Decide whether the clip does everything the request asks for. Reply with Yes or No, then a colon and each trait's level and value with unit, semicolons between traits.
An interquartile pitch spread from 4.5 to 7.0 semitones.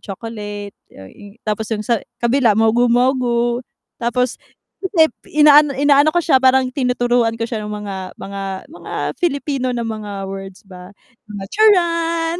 Yes: average, 5.0 semitones